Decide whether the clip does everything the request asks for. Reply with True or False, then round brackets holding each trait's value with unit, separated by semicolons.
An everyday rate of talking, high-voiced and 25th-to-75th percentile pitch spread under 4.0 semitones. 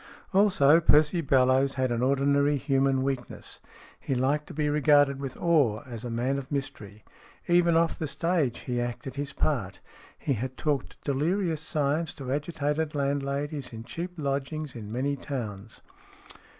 False (150 wpm; 140 Hz; 2.7 semitones)